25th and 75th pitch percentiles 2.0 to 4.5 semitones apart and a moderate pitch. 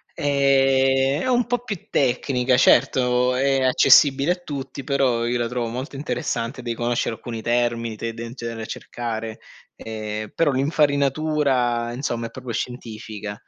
No: average, 2.8 semitones; low, 125 Hz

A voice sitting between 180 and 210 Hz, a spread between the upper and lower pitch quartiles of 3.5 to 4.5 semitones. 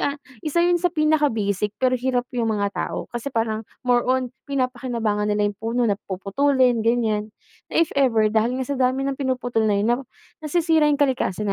No: high, 245 Hz; average, 4.1 semitones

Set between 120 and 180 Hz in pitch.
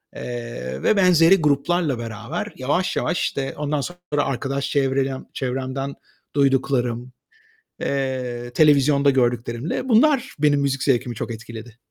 Yes: low, 135 Hz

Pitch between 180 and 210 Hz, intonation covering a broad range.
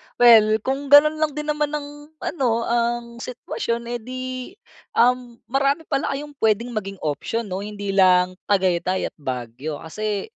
No: high, 235 Hz; wide, 5.7 semitones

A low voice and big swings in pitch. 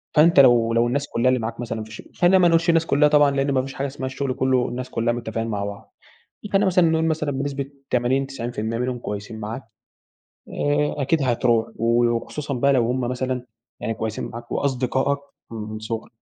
No: low, 130 Hz; average, 3.4 semitones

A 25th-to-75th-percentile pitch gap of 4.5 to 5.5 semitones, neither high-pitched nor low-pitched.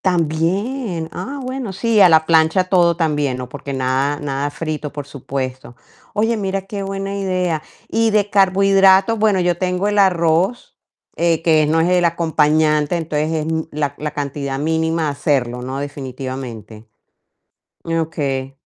Yes: average, 4.9 semitones; medium, 160 Hz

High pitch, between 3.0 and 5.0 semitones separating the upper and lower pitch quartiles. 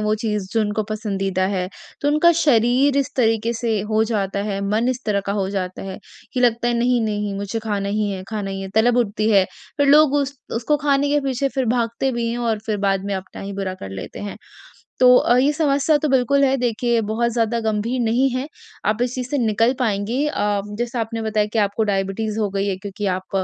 Yes: high, 225 Hz; average, 3.7 semitones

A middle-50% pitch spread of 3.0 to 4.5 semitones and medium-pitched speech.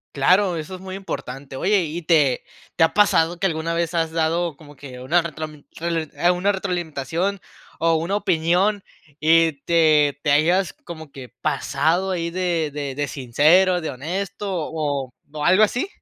Yes: average, 3.3 semitones; medium, 165 Hz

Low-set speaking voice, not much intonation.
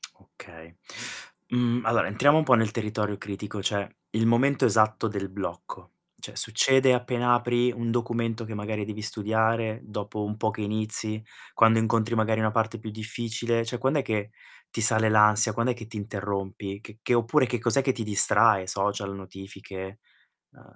Yes: low, 110 Hz; narrow, 2.1 semitones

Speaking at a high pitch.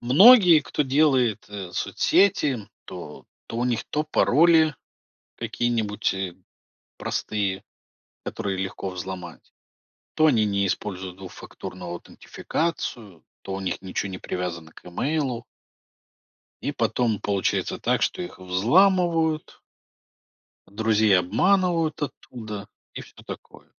No: low, 110 Hz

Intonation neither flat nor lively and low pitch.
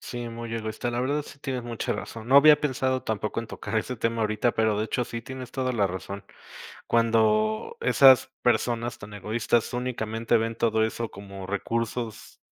No: narrow, 2.2 semitones; low, 115 Hz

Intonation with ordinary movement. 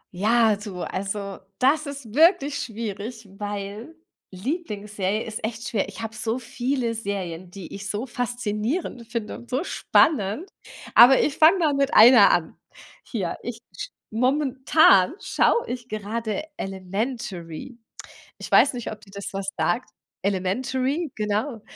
Yes: average, 4.4 semitones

